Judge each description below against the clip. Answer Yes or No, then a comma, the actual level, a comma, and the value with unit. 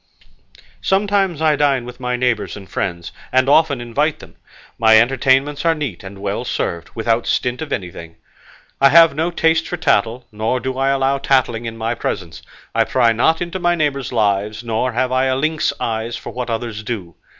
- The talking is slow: No, average, 185 wpm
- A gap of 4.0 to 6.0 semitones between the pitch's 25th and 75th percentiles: Yes, average, 4.5 semitones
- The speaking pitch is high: No, low, 125 Hz